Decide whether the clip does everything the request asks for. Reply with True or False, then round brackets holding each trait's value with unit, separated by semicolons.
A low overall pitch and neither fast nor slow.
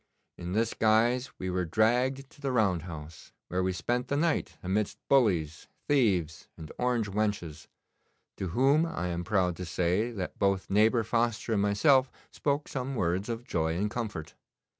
True (105 Hz; 165 wpm)